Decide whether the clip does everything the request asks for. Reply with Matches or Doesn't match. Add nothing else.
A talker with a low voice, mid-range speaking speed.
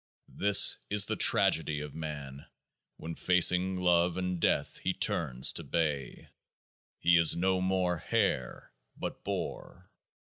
Doesn't match